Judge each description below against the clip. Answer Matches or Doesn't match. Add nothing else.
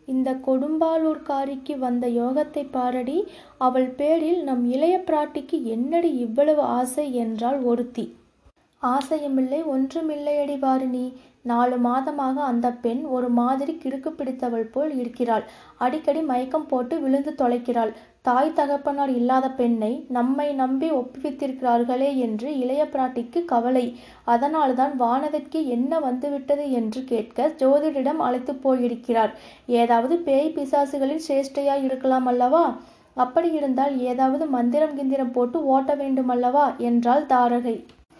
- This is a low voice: Doesn't match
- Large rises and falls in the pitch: Doesn't match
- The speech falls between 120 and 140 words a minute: Doesn't match